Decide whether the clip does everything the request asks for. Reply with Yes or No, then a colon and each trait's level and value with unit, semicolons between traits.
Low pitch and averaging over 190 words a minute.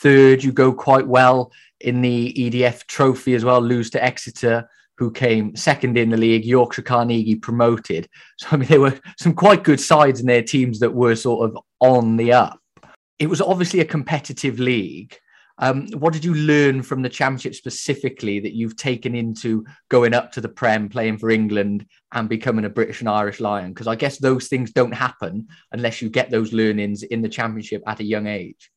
Yes: low, 120 Hz; average, 200 wpm